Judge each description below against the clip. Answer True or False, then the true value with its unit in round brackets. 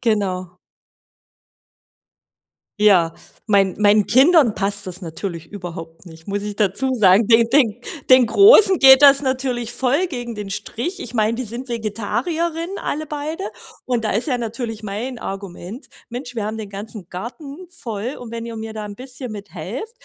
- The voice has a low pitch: False (230 Hz)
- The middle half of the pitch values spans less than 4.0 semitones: False (4.5 semitones)